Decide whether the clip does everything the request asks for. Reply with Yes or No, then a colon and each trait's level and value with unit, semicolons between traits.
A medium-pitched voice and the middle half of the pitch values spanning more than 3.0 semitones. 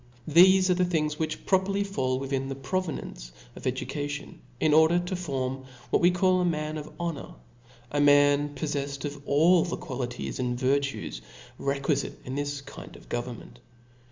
Yes: medium, 145 Hz; average, 4.1 semitones